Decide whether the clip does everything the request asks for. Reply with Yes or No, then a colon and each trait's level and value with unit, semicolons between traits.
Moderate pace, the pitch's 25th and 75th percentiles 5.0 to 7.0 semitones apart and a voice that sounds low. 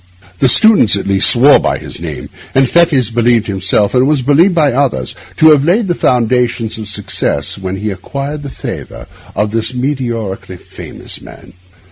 Yes: average, 175 wpm; wide, 5.4 semitones; low, 125 Hz